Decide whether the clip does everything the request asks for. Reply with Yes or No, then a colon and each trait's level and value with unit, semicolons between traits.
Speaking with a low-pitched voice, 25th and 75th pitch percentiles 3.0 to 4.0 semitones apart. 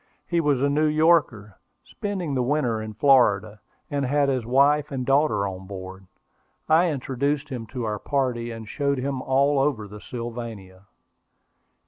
No: low, 130 Hz; average, 4.8 semitones